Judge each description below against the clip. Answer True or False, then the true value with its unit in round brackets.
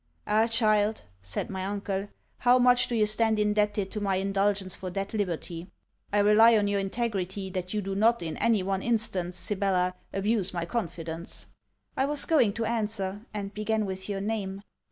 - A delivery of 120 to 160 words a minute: False (175 wpm)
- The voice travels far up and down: False (2.5 semitones)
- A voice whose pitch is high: True (205 Hz)